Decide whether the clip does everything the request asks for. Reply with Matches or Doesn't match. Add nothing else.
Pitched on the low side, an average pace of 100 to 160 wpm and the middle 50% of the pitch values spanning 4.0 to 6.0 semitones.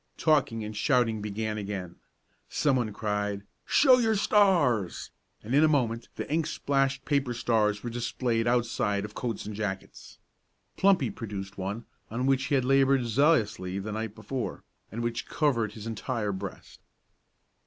Matches